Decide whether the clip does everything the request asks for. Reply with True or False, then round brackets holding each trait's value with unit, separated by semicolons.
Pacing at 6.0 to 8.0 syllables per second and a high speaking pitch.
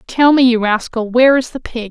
False (5.5 syllables/s; 240 Hz)